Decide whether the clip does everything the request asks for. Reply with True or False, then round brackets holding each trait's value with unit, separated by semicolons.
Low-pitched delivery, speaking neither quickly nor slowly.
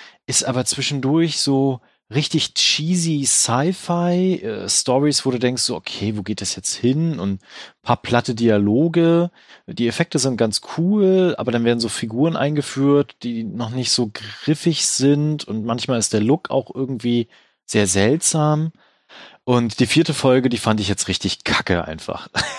True (130 Hz; 160 wpm)